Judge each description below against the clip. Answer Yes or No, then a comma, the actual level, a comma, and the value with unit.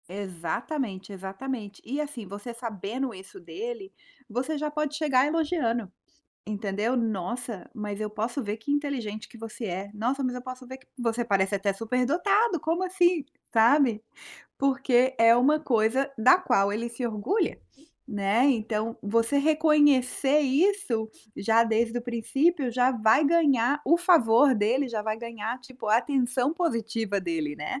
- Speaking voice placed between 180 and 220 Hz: No, high, 240 Hz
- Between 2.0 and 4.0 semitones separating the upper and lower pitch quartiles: No, average, 4.7 semitones